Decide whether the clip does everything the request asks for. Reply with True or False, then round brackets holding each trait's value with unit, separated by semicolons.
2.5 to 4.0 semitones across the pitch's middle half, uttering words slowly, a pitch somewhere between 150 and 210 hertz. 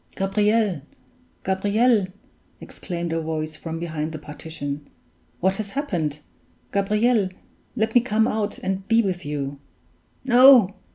False (5.3 semitones; 120 wpm; 190 Hz)